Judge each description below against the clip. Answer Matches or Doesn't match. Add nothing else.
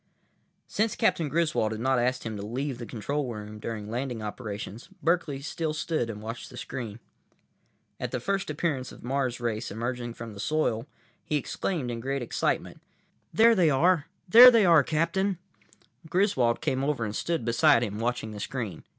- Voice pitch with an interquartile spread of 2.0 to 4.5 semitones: Doesn't match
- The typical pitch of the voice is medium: Doesn't match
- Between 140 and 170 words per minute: Doesn't match